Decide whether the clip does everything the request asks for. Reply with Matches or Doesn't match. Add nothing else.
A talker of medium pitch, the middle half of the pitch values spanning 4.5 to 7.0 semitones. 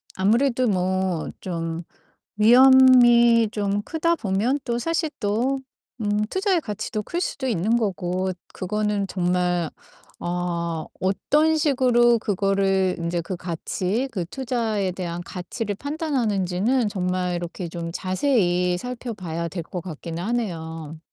Doesn't match